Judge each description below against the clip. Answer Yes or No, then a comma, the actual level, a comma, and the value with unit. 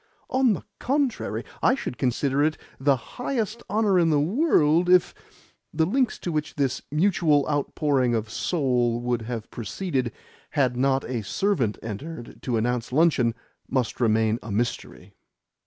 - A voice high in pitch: No, medium, 140 Hz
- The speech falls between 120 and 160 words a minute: Yes, average, 150 wpm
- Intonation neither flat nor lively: No, wide, 6.6 semitones